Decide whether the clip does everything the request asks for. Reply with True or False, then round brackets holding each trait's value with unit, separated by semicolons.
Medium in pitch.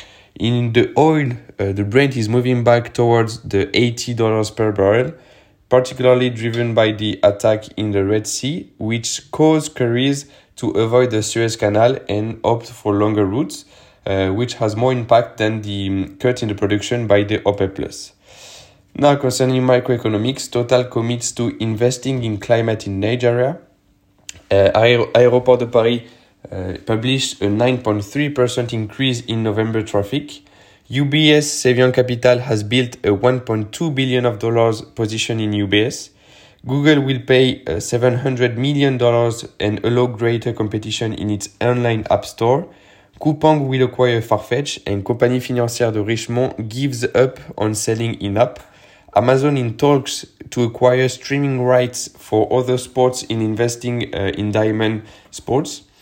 False (120 Hz)